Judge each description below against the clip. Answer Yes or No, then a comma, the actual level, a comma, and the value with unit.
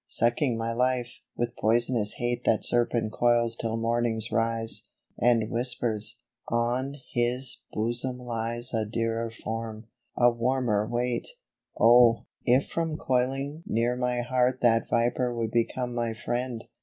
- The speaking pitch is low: Yes, low, 120 Hz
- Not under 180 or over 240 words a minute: No, average, 140 wpm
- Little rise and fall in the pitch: Yes, narrow, 1.4 semitones